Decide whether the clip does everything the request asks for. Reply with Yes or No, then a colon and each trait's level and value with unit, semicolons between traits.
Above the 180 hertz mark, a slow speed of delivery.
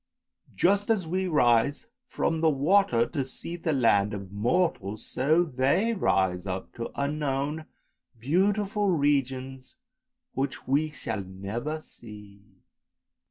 No: medium, 140 Hz; slow, 115 wpm